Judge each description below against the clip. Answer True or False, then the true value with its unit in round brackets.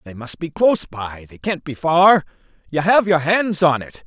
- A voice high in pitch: False (155 Hz)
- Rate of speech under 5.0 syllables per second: True (4.7 syllables/s)